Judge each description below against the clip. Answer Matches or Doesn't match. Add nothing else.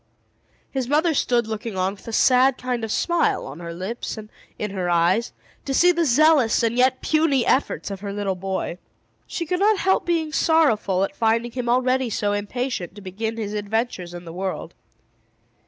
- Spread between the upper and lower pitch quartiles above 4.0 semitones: Matches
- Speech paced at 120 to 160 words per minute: Doesn't match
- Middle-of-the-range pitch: Doesn't match